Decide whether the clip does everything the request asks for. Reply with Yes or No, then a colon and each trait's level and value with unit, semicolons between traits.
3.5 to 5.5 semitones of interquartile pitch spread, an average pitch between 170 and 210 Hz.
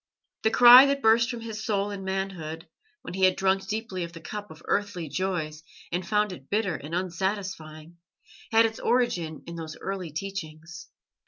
Yes: average, 4.0 semitones; high, 190 Hz